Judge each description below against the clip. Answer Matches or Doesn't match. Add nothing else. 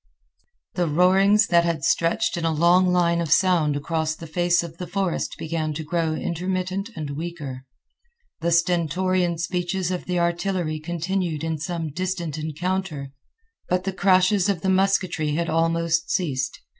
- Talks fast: Doesn't match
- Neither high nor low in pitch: Matches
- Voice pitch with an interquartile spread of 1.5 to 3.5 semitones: Matches